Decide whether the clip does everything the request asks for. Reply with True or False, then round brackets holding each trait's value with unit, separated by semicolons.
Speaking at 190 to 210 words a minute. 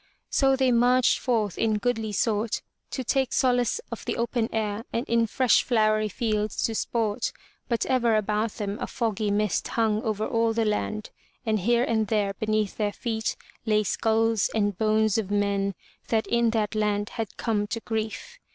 False (175 wpm)